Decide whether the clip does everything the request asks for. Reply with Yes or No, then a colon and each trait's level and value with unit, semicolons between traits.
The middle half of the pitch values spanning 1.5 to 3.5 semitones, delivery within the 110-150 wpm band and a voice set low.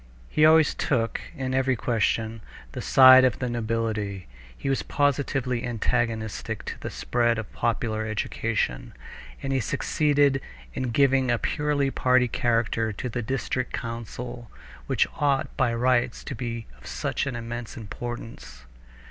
Yes: narrow, 2.6 semitones; average, 140 wpm; low, 120 Hz